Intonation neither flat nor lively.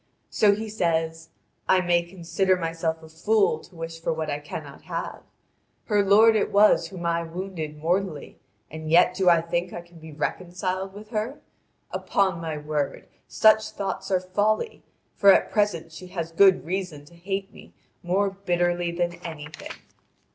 Yes: average, 3.1 semitones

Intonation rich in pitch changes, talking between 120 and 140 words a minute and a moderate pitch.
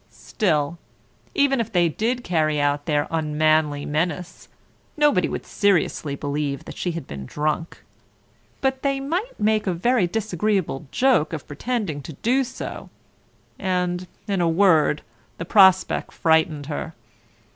Yes: wide, 6.1 semitones; slow, 135 wpm; medium, 170 Hz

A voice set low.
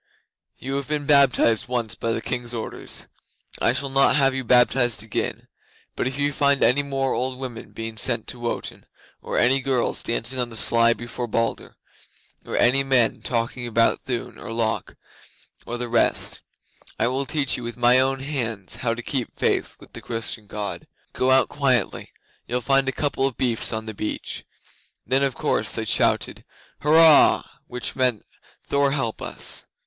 Yes: low, 125 Hz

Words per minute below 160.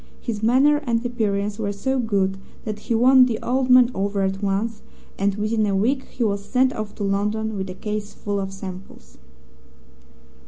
No: average, 185 wpm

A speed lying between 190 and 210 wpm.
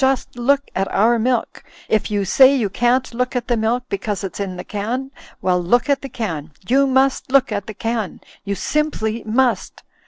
Yes: average, 200 wpm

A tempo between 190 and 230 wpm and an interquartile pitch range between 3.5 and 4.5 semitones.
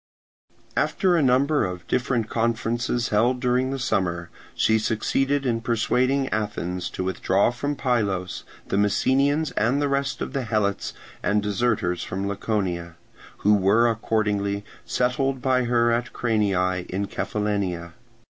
No: slow, 135 wpm; average, 4.2 semitones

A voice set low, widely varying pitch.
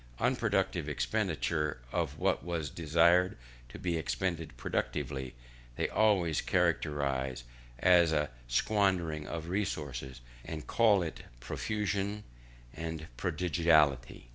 No: very low, 80 Hz; average, 4.3 semitones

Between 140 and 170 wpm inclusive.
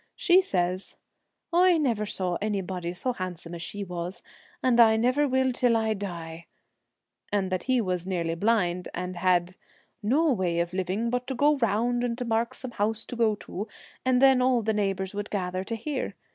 No: average, 195 wpm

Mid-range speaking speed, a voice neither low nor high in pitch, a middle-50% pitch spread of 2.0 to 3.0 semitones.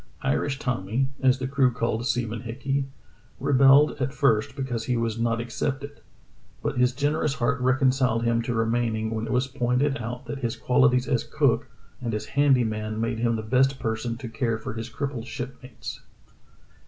No: average, 180 wpm; low, 125 Hz; average, 2.7 semitones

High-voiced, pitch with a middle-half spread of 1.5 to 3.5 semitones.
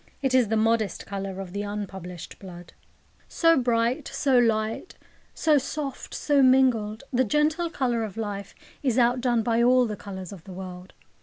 No: high, 230 Hz; average, 4.5 semitones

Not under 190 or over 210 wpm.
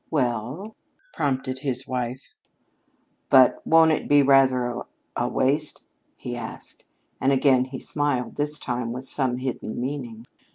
No: slow, 135 wpm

